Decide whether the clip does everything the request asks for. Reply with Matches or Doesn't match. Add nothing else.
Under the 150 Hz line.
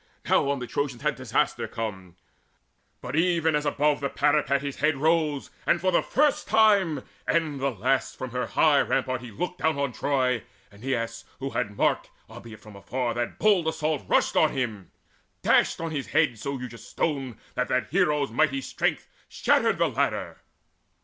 Matches